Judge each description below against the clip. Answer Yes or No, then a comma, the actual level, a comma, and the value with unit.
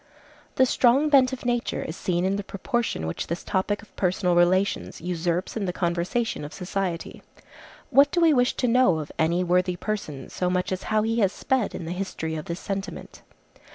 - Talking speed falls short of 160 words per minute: No, average, 195 wpm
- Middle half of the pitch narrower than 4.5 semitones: No, average, 5.0 semitones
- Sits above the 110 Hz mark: Yes, high, 190 Hz